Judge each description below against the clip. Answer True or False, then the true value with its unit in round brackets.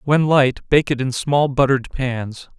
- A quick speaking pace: False (185 wpm)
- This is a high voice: False (135 Hz)